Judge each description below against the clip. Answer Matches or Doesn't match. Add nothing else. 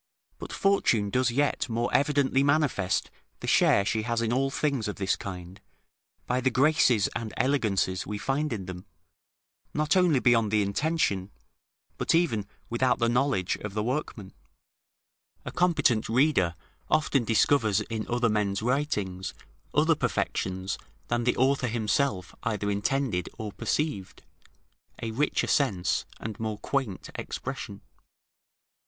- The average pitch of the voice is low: Matches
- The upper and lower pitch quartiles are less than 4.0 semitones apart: Doesn't match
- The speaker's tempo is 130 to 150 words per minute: Matches